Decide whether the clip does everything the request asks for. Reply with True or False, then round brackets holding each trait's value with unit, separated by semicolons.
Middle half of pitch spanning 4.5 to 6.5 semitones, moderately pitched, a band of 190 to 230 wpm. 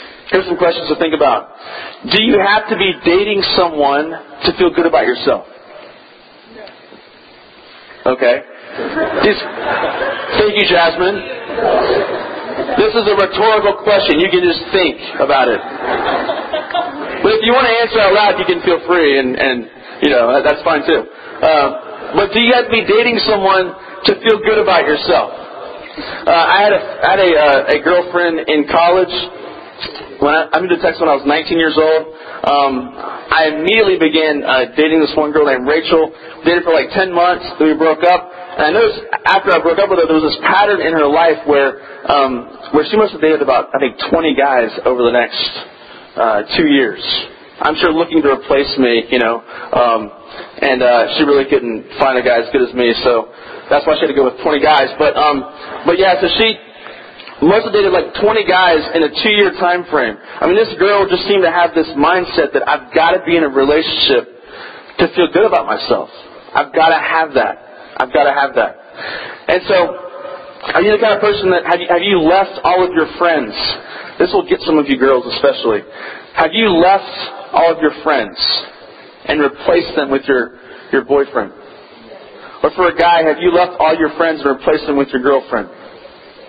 True (4.9 semitones; 170 Hz; 195 wpm)